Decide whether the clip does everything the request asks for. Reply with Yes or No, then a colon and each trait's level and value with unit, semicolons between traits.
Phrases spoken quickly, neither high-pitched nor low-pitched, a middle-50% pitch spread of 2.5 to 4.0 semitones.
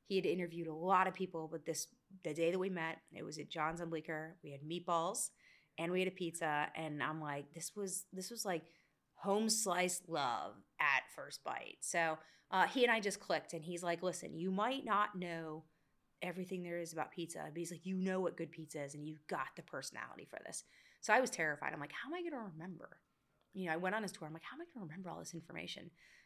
Yes: fast, 245 wpm; medium, 175 Hz; average, 2.9 semitones